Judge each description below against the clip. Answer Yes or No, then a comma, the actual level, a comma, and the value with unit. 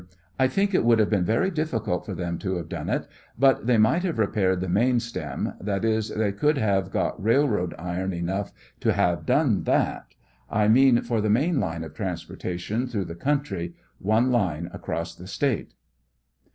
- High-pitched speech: No, low, 105 Hz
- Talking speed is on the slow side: No, average, 185 wpm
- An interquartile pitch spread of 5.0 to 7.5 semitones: Yes, wide, 5.4 semitones